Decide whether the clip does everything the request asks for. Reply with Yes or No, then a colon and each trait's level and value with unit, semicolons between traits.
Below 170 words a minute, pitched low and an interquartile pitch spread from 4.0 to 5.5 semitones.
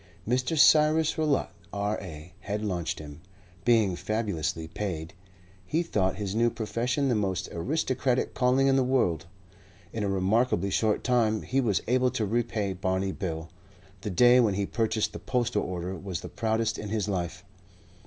Yes: average, 160 wpm; low, 105 Hz; average, 4.8 semitones